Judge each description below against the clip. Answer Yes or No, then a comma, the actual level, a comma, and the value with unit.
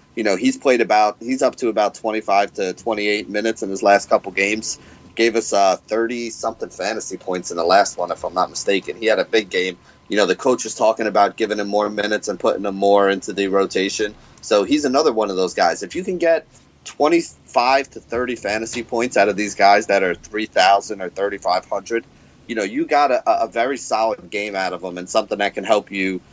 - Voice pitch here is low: Yes, low, 105 Hz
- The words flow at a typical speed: No, fast, 225 wpm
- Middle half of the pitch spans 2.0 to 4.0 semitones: Yes, average, 2.7 semitones